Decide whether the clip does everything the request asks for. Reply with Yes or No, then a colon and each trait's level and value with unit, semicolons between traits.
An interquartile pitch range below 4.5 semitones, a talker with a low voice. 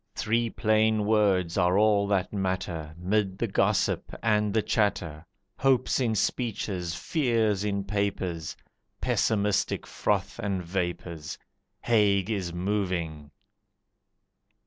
Yes: average, 3.2 semitones; low, 100 Hz